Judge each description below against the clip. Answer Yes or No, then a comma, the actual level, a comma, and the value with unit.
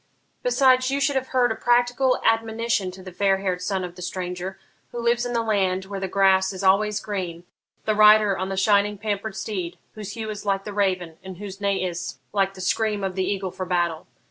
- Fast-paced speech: Yes, fast, 220 wpm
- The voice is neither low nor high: No, high, 200 Hz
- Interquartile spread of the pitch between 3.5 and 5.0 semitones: No, average, 2.7 semitones